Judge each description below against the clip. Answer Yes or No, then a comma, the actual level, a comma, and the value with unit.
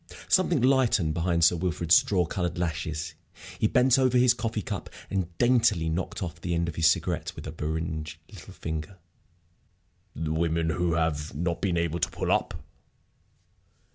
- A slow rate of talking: No, average, 165 wpm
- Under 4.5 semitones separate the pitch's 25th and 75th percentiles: Yes, average, 3.5 semitones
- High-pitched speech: No, very low, 85 Hz